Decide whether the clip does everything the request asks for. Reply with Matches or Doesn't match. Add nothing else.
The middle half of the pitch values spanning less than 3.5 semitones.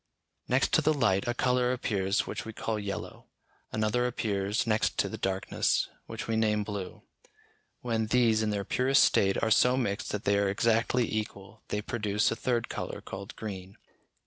Matches